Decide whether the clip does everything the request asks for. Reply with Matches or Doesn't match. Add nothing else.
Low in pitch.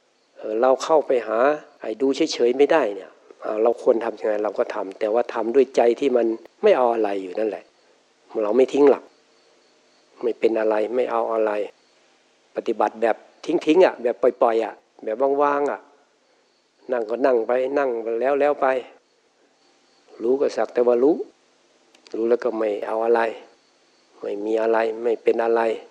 Matches